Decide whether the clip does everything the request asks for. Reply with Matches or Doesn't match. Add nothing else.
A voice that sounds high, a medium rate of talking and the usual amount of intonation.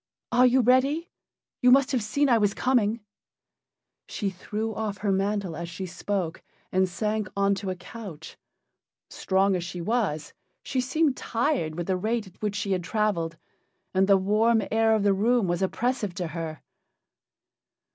Matches